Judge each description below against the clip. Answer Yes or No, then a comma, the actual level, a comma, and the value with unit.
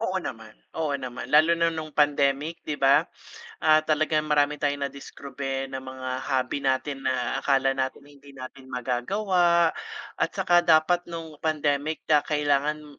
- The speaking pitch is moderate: Yes, medium, 145 Hz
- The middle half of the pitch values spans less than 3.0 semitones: Yes, narrow, 2.6 semitones